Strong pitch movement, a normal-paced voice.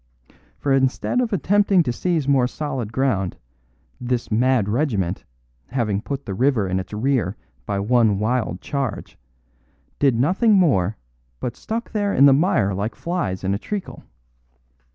Yes: wide, 6.0 semitones; average, 145 wpm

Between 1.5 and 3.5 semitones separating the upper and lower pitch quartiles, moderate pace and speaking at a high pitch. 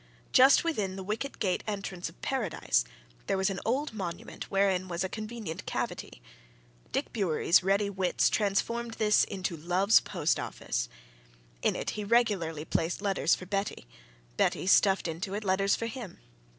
Yes: average, 2.9 semitones; average, 155 wpm; high, 195 Hz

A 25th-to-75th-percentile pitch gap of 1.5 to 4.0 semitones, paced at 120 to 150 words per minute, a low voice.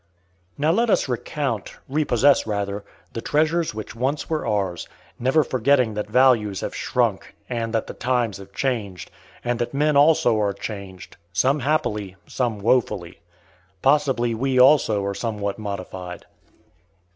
No: average, 5.1 semitones; average, 140 wpm; low, 120 Hz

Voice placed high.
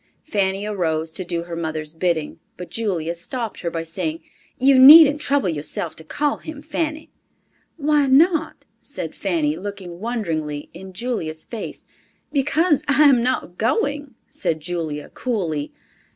Yes: high, 200 Hz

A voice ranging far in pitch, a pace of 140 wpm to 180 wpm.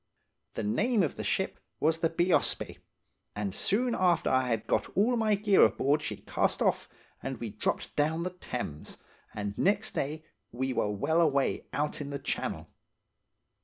Yes: wide, 6.3 semitones; average, 165 wpm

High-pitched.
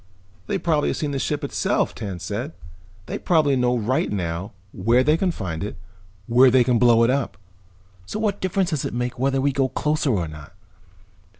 No: low, 125 Hz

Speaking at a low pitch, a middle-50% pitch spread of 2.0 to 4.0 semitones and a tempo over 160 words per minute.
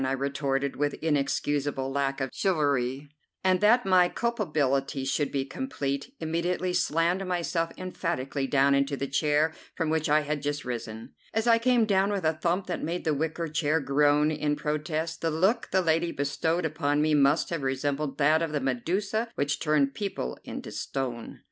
No: medium, 150 Hz; average, 3.6 semitones; average, 175 wpm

